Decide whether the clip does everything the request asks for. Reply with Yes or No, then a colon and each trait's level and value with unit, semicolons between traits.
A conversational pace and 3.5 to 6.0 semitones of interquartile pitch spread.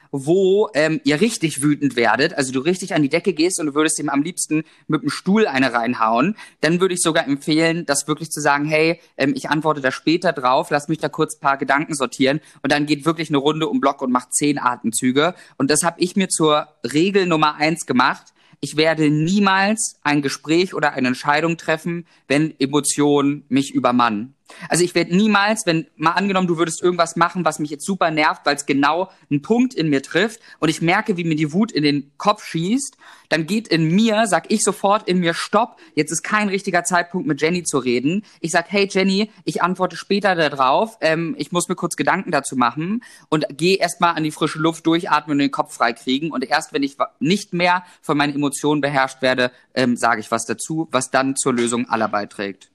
No: fast, 215 wpm; average, 3.9 semitones